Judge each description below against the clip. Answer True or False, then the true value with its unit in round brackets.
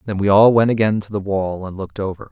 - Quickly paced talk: True (285 wpm)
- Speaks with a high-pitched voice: False (100 Hz)